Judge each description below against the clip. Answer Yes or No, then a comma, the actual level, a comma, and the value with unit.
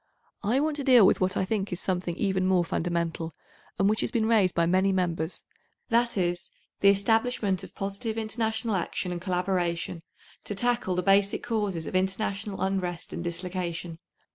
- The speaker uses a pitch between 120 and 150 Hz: No, high, 190 Hz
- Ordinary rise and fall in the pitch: Yes, average, 3.5 semitones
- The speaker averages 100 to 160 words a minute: No, average, 170 wpm